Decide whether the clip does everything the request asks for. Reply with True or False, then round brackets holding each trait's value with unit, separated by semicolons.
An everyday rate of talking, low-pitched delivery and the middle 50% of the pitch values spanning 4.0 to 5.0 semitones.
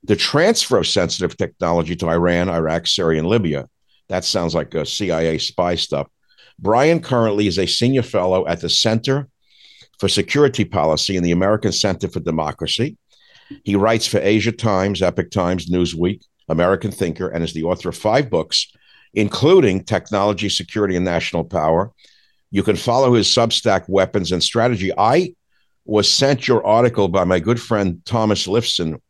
True (160 wpm; 100 Hz; 4.3 semitones)